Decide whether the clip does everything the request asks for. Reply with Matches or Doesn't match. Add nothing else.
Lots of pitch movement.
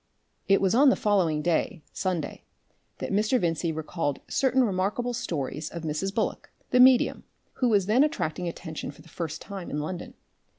Matches